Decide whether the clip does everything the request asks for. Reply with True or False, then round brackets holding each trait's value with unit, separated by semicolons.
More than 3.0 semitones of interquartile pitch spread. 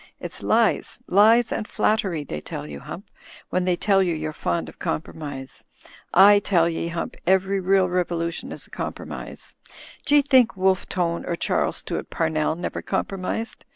True (3.4 semitones)